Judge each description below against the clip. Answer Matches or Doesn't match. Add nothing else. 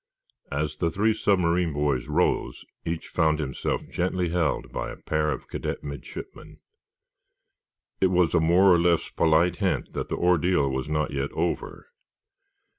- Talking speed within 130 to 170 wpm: Matches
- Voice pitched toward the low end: Matches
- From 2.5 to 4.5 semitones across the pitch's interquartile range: Matches